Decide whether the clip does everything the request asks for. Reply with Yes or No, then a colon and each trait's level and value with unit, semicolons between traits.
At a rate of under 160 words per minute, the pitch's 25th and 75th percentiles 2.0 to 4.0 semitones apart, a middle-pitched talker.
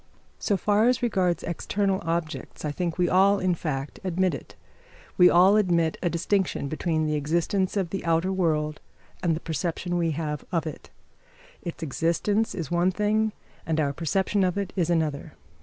No: average, 175 wpm; average, 3.0 semitones; medium, 175 Hz